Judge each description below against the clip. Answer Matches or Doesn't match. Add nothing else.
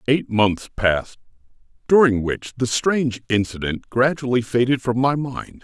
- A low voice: Matches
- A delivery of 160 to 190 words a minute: Doesn't match